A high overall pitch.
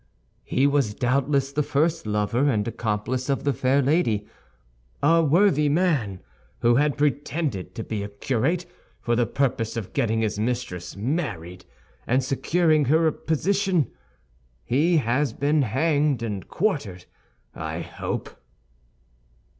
No: low, 135 Hz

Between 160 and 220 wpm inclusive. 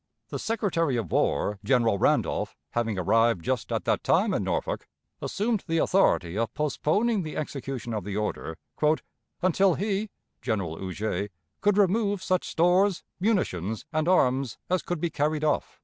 No: average, 150 wpm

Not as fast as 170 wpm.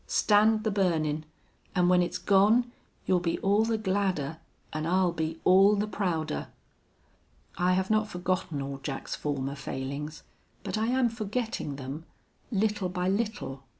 Yes: average, 150 wpm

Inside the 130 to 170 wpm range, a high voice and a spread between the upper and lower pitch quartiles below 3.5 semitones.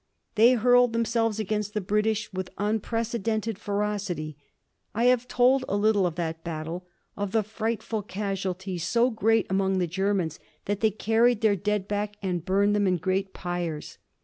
Yes: average, 160 wpm; high, 205 Hz; average, 2.9 semitones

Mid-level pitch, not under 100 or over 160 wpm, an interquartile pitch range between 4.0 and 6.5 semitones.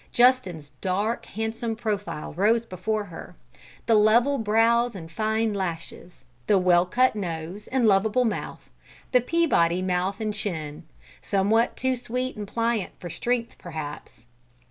No: high, 210 Hz; slow, 135 wpm; average, 4.3 semitones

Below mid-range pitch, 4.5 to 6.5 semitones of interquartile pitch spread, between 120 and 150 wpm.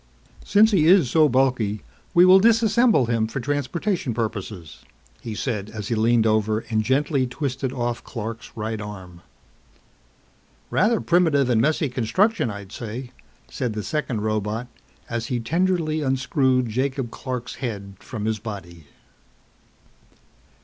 Yes: low, 120 Hz; average, 5.2 semitones; slow, 135 wpm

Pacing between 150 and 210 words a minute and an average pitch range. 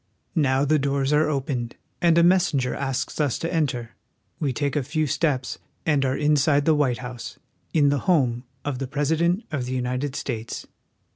Yes: average, 180 wpm; average, 3.1 semitones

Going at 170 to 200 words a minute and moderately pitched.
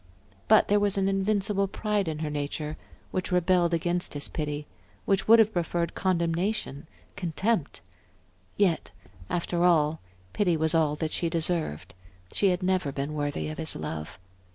No: average, 155 wpm; medium, 170 Hz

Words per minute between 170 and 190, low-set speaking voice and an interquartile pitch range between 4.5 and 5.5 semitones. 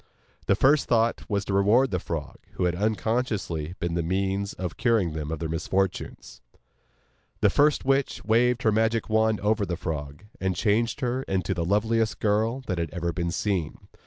Yes: average, 180 wpm; low, 100 Hz; average, 4.8 semitones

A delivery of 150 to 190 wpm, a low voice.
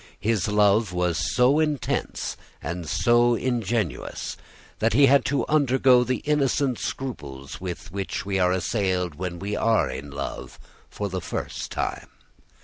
No: slow, 135 wpm; low, 105 Hz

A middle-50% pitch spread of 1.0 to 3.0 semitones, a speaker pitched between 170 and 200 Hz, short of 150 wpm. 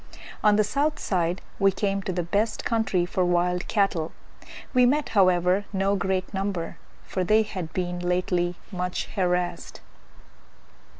Yes: narrow, 2.4 semitones; medium, 185 Hz; average, 140 wpm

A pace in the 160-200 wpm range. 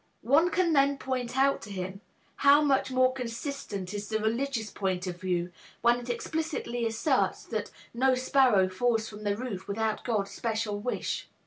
Yes: average, 165 wpm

